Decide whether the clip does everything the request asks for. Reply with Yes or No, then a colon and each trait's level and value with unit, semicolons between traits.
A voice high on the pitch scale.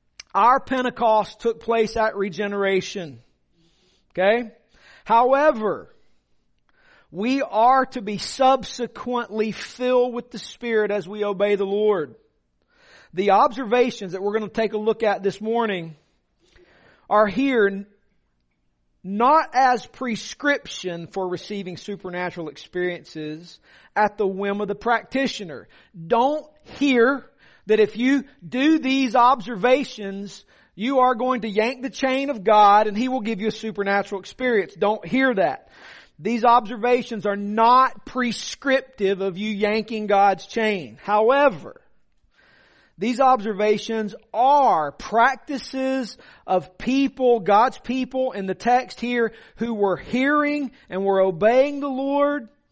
Yes: high, 220 Hz